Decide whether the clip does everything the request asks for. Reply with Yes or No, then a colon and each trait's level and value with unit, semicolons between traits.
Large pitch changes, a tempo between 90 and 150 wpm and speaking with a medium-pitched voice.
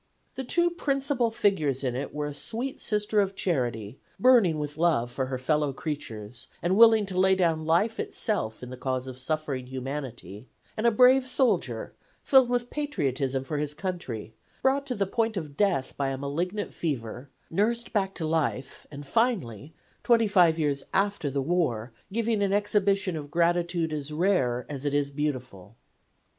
No: wide, 7.5 semitones; average, 170 wpm; medium, 160 Hz